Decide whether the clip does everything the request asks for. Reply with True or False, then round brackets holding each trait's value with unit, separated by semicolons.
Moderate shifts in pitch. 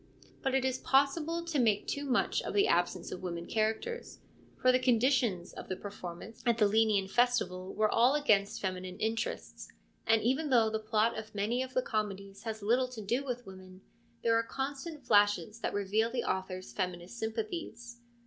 True (4.3 semitones)